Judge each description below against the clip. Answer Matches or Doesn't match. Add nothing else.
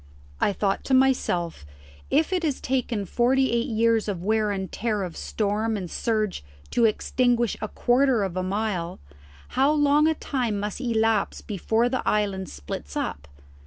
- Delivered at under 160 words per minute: Doesn't match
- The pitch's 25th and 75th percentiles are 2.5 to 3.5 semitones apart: Doesn't match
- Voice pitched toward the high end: Matches